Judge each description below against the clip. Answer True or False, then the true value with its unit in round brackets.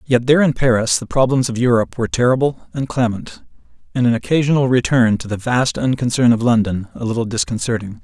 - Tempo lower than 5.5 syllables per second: False (6.1 syllables/s)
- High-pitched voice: False (120 Hz)